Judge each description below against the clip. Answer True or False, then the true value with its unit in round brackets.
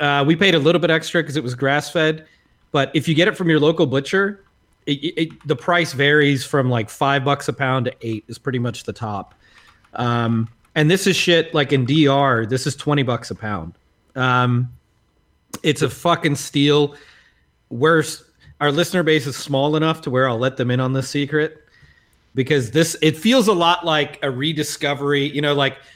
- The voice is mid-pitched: True (145 Hz)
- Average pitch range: True (3.3 semitones)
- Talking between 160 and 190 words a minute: False (200 wpm)